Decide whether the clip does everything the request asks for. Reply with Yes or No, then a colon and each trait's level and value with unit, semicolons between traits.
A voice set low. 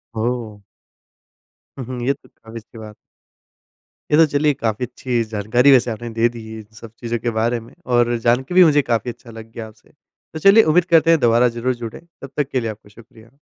Yes: low, 120 Hz